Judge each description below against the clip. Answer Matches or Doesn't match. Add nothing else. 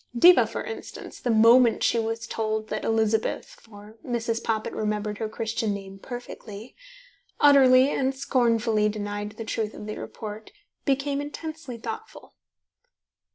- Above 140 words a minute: Doesn't match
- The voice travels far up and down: Doesn't match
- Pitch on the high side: Matches